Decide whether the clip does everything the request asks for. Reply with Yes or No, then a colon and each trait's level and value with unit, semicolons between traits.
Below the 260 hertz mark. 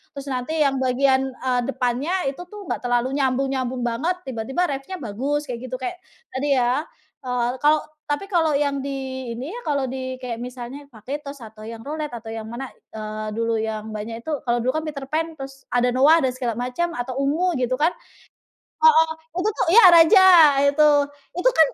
No: very high, 265 Hz